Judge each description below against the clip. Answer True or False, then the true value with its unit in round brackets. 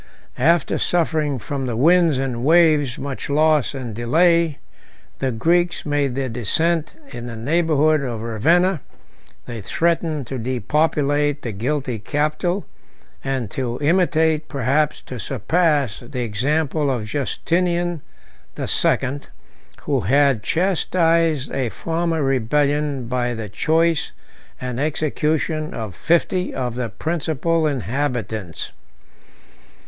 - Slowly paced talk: True (115 wpm)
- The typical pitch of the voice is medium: True (145 Hz)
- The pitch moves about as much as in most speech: True (4.5 semitones)